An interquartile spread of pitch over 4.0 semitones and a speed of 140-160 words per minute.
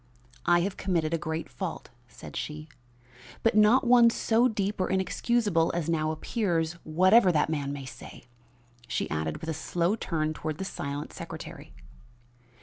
Yes: average, 4.7 semitones; average, 155 wpm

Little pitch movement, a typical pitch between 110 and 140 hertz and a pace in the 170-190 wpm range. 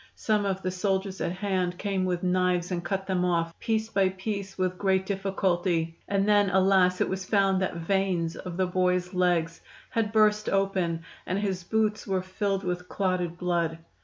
No: narrow, 1.6 semitones; medium, 185 Hz; average, 180 wpm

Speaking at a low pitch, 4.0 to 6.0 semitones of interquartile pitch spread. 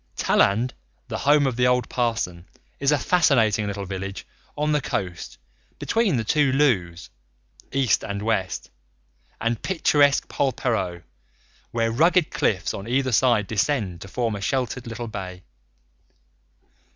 Yes: low, 115 Hz; wide, 5.6 semitones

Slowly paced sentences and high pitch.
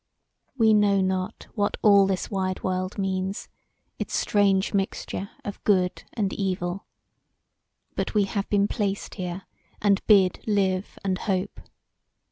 Yes: slow, 130 wpm; high, 195 Hz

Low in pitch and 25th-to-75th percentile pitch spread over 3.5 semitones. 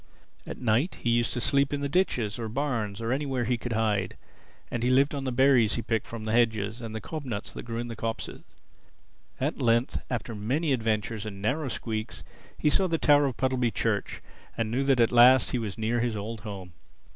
No: low, 120 Hz; average, 3.2 semitones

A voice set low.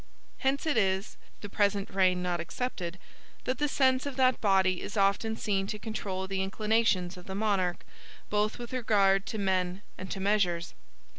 No: high, 200 Hz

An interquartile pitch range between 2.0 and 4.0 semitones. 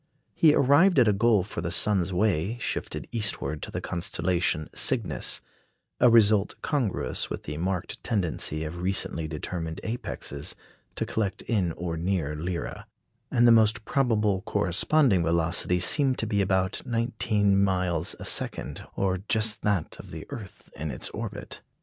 No: average, 4.6 semitones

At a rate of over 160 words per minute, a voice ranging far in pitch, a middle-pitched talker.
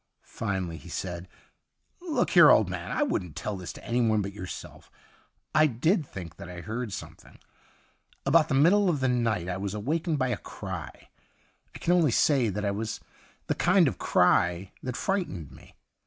No: average, 185 wpm; wide, 8.1 semitones; low, 115 Hz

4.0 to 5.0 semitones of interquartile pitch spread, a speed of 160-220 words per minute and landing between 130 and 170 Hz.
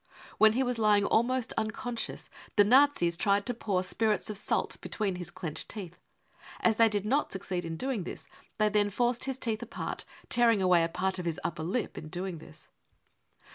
No: average, 4.3 semitones; average, 190 wpm; high, 210 Hz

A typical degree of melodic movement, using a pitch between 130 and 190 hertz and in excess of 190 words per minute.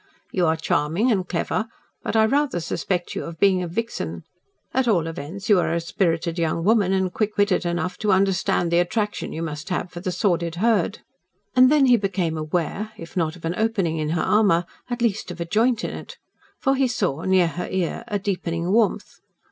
Yes: average, 4.2 semitones; medium, 185 Hz; fast, 205 wpm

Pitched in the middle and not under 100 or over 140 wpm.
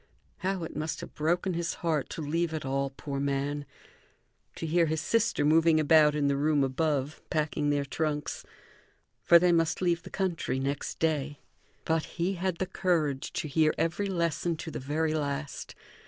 No: medium, 155 Hz; average, 175 wpm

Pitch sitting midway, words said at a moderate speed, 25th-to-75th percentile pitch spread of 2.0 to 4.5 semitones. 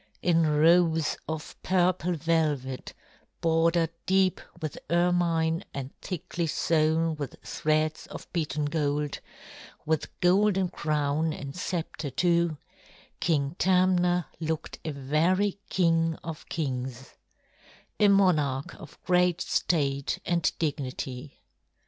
No: medium, 160 Hz; slow, 105 wpm; average, 3.0 semitones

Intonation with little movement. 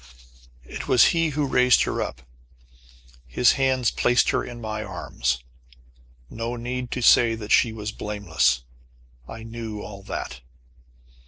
No: average, 3.1 semitones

